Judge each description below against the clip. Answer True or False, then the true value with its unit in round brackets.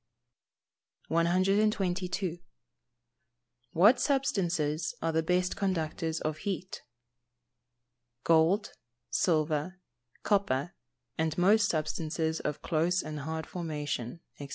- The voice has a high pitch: False (165 Hz)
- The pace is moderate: False (85 wpm)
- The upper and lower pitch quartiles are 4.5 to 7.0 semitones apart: False (3.0 semitones)